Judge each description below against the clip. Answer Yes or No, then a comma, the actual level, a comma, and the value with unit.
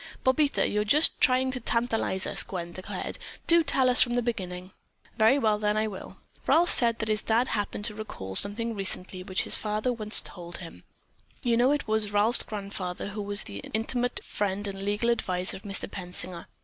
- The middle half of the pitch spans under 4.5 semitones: Yes, average, 3.6 semitones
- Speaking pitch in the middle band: No, high, 210 Hz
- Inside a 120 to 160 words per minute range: No, average, 195 wpm